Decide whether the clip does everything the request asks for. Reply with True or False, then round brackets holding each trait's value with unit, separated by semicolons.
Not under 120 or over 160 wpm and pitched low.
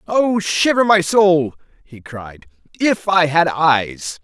False (140 wpm; 160 Hz)